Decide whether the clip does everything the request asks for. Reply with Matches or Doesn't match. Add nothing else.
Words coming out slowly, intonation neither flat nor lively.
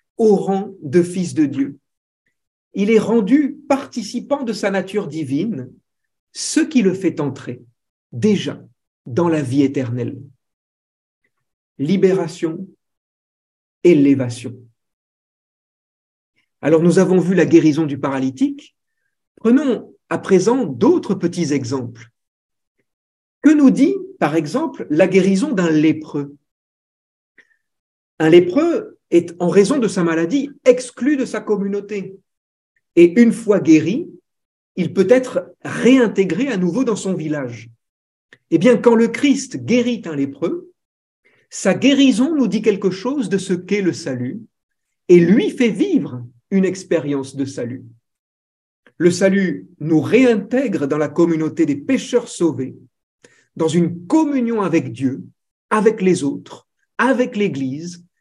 Doesn't match